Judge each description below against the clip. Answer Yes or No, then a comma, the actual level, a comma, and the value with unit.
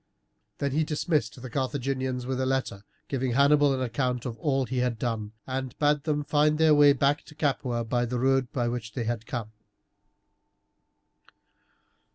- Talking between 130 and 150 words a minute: No, average, 170 wpm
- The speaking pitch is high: No, low, 130 Hz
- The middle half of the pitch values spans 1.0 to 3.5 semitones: Yes, average, 2.9 semitones